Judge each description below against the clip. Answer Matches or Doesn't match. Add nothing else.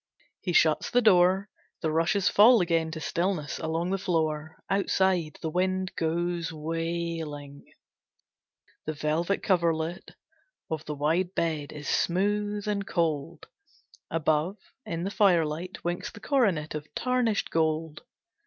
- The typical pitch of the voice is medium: Matches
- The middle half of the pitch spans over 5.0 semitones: Doesn't match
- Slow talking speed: Matches